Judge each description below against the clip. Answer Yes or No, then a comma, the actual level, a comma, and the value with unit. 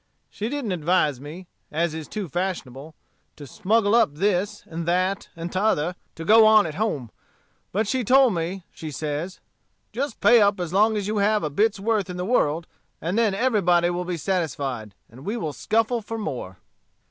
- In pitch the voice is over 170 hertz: Yes, medium, 185 Hz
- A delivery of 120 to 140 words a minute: No, average, 185 wpm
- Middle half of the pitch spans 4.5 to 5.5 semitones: Yes, average, 5.0 semitones